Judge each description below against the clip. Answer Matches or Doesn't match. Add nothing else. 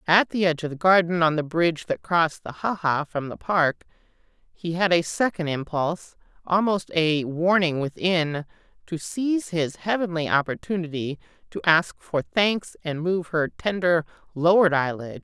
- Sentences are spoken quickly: Doesn't match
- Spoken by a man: Doesn't match